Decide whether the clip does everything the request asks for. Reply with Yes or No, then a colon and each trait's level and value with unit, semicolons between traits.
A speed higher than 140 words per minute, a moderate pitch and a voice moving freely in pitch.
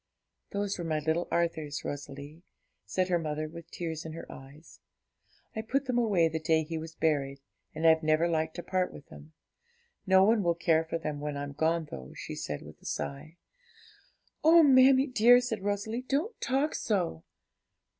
No: average, 180 wpm; medium, 165 Hz; average, 4.8 semitones